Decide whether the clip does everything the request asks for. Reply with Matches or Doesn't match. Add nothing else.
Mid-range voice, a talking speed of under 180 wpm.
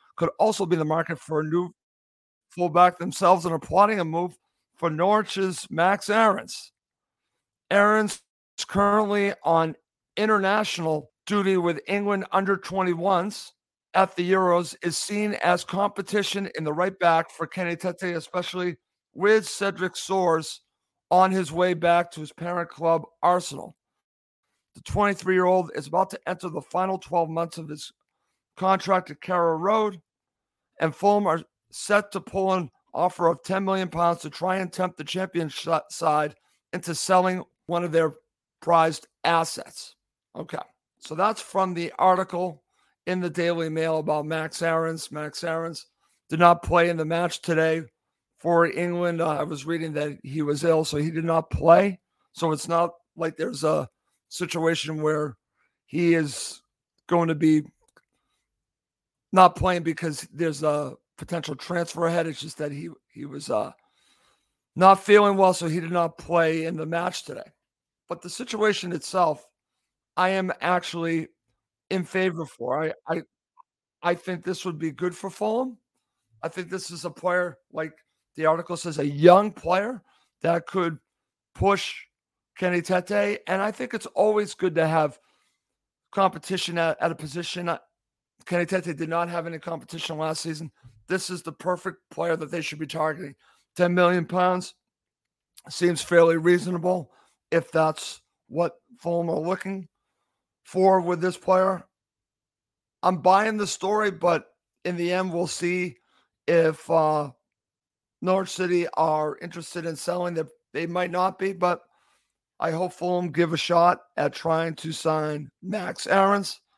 Matches